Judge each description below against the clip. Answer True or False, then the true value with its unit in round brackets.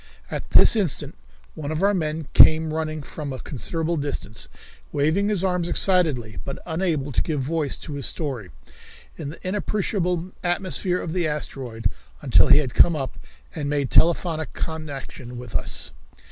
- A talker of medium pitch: True (155 Hz)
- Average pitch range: True (3.7 semitones)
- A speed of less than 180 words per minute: True (160 wpm)